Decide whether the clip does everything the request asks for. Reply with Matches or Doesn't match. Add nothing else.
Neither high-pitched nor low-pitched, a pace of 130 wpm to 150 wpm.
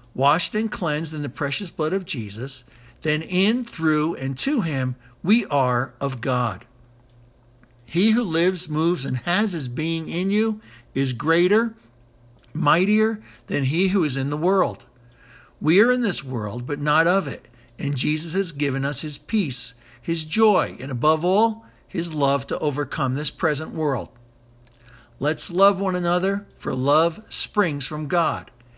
Doesn't match